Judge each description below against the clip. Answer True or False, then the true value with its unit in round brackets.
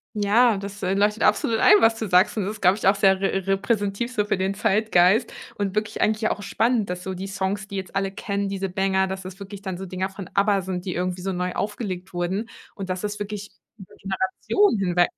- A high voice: True (195 Hz)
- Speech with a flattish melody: True (1.7 semitones)